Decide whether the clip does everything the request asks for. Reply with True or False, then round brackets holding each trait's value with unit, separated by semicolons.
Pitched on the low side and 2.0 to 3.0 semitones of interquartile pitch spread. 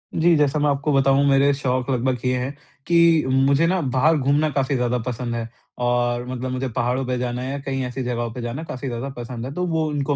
True (130 Hz; 2.4 semitones)